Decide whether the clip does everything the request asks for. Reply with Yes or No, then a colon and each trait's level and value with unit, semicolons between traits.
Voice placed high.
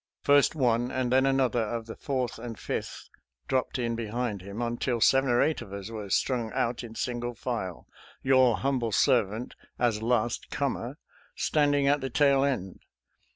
No: low, 120 Hz